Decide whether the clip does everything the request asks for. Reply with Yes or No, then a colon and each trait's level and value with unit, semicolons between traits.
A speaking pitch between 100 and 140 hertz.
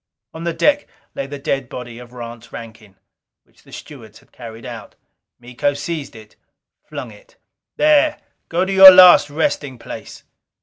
Yes: low, 135 Hz